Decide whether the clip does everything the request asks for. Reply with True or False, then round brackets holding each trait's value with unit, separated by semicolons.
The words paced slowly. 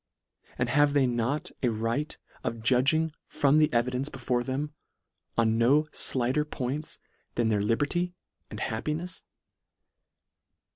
True (130 wpm)